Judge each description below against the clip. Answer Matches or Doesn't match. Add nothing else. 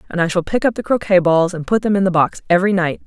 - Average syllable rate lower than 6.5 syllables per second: Doesn't match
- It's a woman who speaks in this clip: Matches